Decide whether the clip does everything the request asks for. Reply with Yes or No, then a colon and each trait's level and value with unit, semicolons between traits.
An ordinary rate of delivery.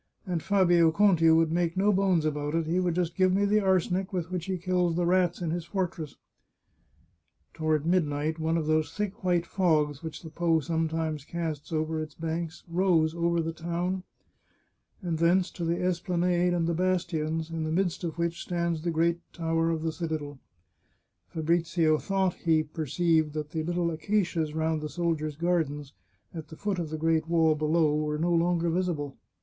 Yes: average, 185 wpm